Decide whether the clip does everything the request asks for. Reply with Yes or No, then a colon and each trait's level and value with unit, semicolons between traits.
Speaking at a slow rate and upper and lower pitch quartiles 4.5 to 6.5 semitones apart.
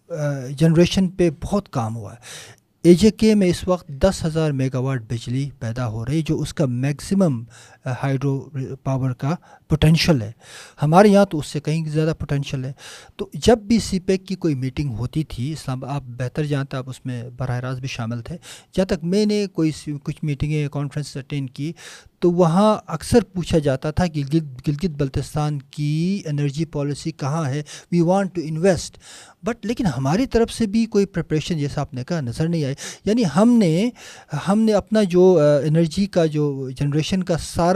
No: average, 185 wpm; average, 4.8 semitones